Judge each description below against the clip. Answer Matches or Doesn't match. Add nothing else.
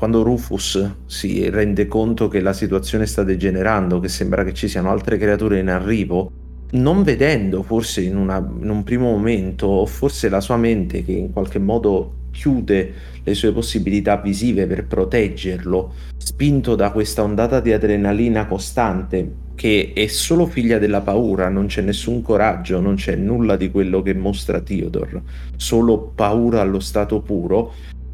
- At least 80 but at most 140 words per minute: Doesn't match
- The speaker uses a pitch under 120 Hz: Matches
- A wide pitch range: Doesn't match